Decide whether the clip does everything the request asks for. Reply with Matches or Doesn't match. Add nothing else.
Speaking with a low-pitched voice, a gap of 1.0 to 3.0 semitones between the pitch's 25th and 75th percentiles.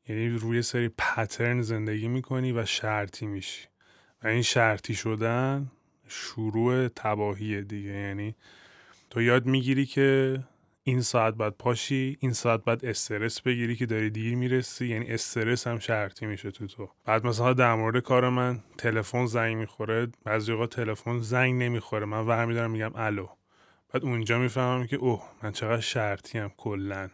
Matches